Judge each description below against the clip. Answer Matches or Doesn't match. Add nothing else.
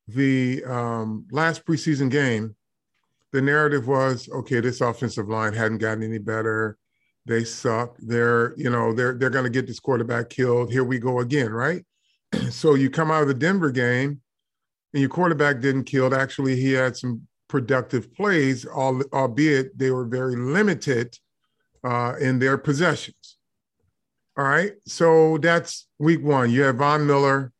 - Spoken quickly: Doesn't match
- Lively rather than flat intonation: Doesn't match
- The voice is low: Matches